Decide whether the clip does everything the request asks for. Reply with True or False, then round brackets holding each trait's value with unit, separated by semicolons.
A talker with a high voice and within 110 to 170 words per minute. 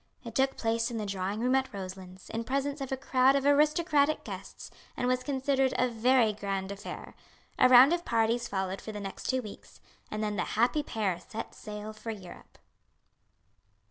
False (230 Hz; 185 wpm)